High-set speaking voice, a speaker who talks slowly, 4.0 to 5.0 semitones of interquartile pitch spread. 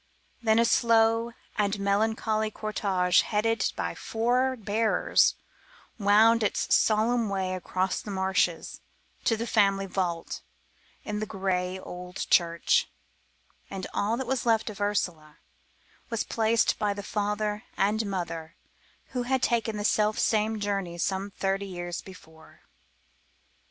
No: high, 205 Hz; slow, 130 wpm; average, 2.8 semitones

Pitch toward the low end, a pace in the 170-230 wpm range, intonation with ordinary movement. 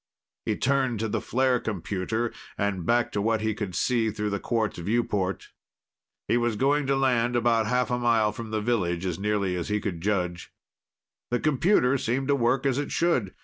Yes: low, 115 Hz; average, 190 wpm; average, 3.4 semitones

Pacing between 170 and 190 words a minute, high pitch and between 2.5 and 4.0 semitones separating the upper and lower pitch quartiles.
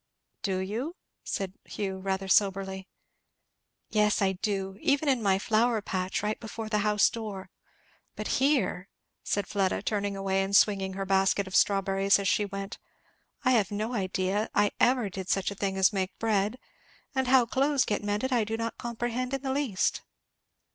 Yes: average, 175 wpm; high, 205 Hz; average, 3.0 semitones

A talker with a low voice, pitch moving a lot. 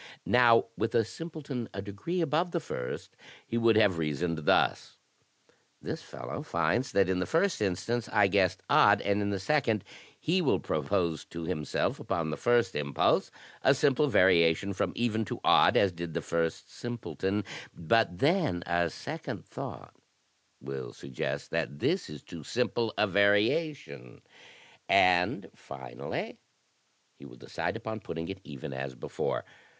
Yes: low, 100 Hz; wide, 6.2 semitones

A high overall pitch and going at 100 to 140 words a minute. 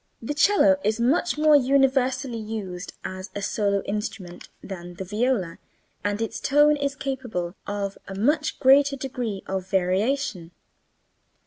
Yes: high, 225 Hz; slow, 135 wpm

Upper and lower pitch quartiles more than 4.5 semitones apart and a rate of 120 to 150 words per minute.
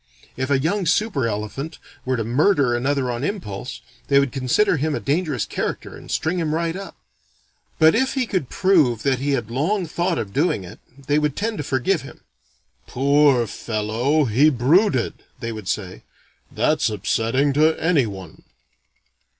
No: average, 5.2 semitones; average, 165 wpm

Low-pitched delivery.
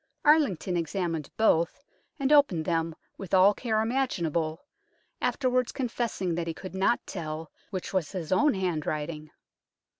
No: medium, 185 Hz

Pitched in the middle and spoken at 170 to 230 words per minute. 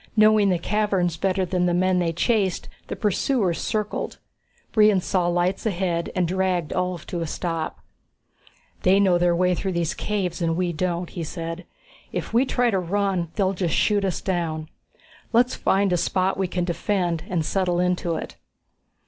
Yes: medium, 180 Hz; average, 175 wpm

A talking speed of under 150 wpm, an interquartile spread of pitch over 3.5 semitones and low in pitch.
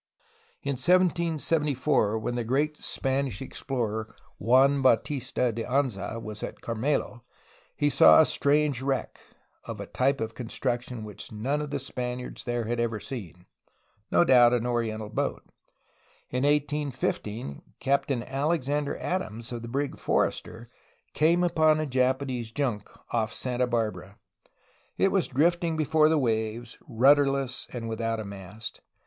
Yes: average, 140 wpm; average, 4.0 semitones; low, 125 Hz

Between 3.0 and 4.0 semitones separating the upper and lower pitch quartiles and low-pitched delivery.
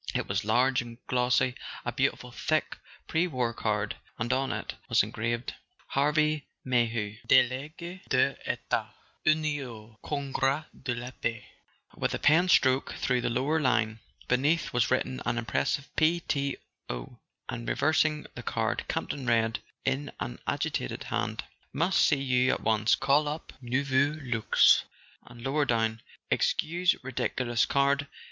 Yes: average, 3.7 semitones; low, 130 Hz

